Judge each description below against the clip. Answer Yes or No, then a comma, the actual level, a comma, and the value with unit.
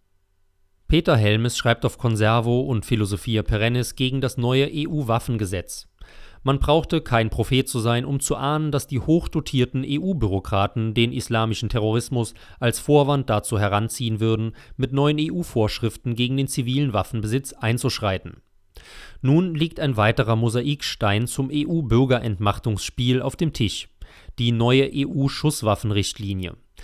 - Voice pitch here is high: No, low, 120 Hz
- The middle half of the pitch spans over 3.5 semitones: Yes, average, 4.2 semitones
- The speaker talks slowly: Yes, slow, 120 wpm